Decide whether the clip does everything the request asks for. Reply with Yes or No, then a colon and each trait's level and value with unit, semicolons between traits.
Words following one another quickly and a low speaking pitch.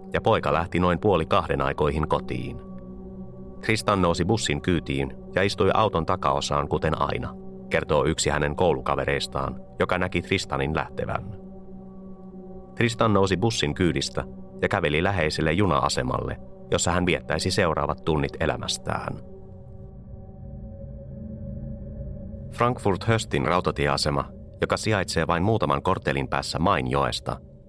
No: average, 105 wpm; very low, 85 Hz